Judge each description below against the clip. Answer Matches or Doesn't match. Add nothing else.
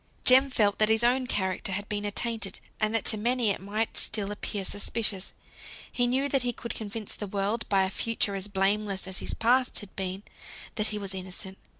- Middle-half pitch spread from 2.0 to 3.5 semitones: Matches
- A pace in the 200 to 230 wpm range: Matches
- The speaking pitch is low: Doesn't match